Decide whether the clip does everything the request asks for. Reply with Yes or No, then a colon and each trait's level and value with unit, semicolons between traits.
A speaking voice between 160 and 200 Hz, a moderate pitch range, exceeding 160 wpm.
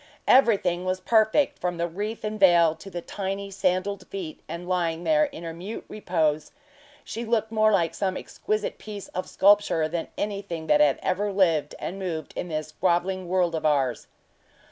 Yes: medium, 185 Hz; average, 3.5 semitones; average, 175 wpm